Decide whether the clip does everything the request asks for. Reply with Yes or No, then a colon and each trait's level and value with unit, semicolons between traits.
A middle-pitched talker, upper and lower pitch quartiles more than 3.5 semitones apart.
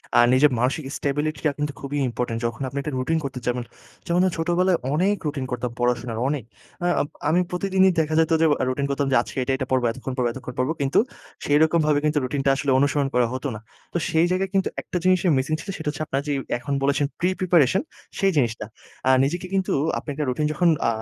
Yes: medium, 145 Hz; average, 4.3 semitones